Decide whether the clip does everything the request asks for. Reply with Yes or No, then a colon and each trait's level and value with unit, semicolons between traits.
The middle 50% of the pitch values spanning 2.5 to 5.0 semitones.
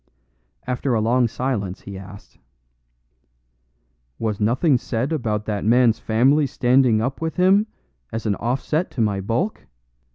Yes: average, 4.0 semitones